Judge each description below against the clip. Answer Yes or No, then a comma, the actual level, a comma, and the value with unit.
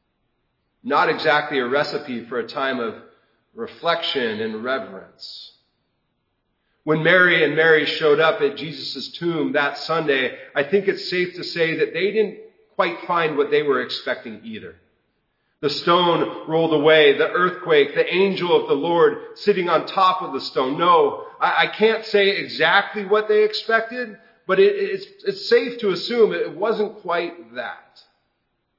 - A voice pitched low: No, high, 210 Hz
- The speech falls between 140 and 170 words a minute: Yes, average, 150 wpm